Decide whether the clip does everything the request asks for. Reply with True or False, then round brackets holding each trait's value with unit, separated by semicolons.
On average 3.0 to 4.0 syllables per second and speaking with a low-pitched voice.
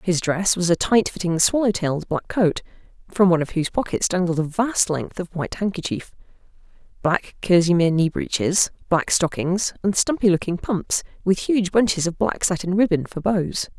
False (3.9 syllables/s; 180 Hz)